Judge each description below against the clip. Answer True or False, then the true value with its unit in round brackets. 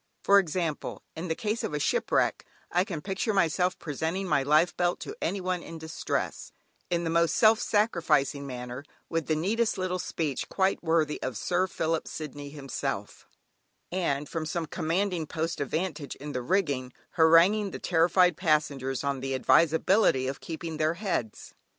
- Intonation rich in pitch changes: False (3.7 semitones)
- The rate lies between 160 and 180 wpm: True (165 wpm)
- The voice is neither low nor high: True (165 Hz)